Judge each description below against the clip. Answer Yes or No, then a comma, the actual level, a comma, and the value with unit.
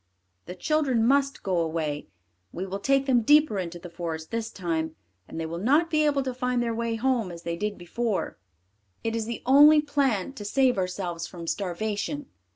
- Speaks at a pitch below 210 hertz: No, high, 225 Hz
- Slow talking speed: No, average, 190 wpm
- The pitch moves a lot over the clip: Yes, wide, 7.2 semitones